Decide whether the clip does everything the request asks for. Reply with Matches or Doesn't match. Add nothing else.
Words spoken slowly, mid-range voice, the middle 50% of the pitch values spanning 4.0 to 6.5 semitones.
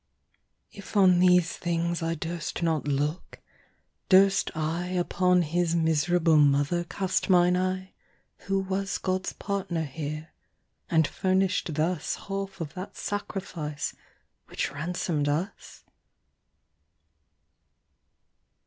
Doesn't match